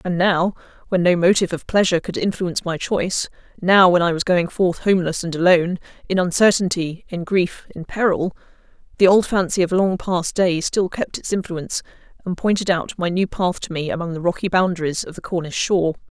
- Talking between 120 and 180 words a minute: No, average, 190 wpm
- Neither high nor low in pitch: Yes, medium, 180 Hz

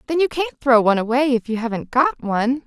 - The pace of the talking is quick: Yes, fast, 245 wpm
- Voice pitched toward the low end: No, very high, 260 Hz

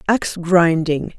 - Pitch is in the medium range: Yes, medium, 175 Hz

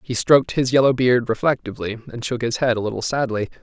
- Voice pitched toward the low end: Yes, low, 120 Hz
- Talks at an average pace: No, fast, 215 wpm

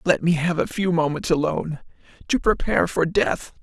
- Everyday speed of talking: Yes, average, 180 wpm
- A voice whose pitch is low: No, medium, 165 Hz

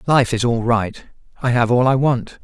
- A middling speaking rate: No, fast, 220 wpm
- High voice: No, low, 120 Hz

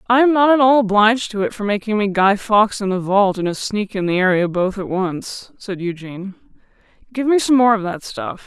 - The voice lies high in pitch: Yes, high, 210 Hz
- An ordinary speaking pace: No, fast, 240 wpm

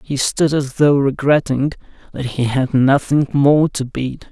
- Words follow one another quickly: No, average, 165 wpm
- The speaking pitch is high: No, medium, 140 Hz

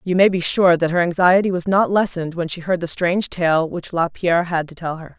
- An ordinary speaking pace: No, fast, 255 wpm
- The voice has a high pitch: No, medium, 175 Hz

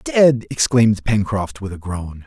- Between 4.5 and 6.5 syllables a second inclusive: No, 4.1 syllables/s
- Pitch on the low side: Yes, low, 110 Hz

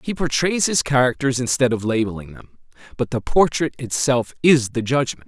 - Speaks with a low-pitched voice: Yes, low, 130 Hz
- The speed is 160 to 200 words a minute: Yes, average, 170 wpm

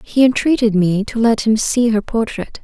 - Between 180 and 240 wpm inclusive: Yes, fast, 205 wpm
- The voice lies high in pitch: Yes, high, 225 Hz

